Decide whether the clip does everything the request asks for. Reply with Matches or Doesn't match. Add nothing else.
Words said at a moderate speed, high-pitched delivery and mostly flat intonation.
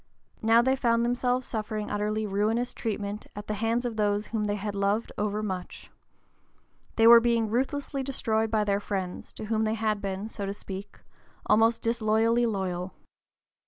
Matches